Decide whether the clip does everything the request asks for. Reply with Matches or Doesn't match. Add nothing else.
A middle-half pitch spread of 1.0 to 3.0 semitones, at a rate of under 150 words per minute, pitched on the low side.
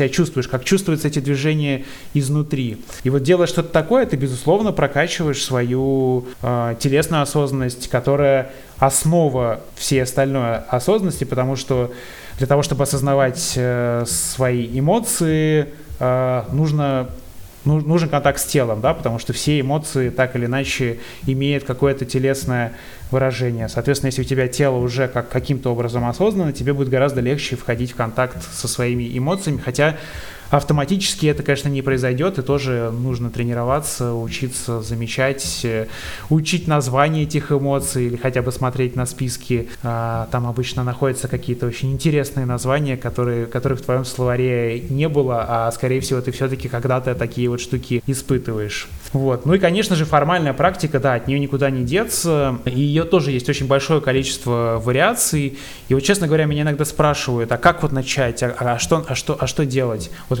Doesn't match